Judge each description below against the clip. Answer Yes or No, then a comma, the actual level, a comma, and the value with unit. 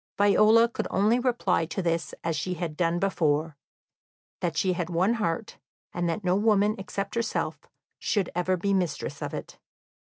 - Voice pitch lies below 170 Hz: No, medium, 185 Hz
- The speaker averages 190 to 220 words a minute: No, average, 165 wpm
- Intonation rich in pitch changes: No, average, 3.7 semitones